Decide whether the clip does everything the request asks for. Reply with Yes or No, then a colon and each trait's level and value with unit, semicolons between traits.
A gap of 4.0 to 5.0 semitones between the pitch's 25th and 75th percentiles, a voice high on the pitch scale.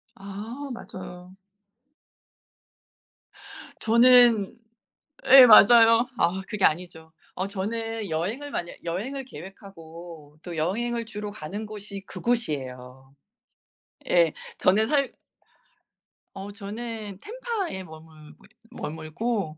No: wide, 5.5 semitones; high, 200 Hz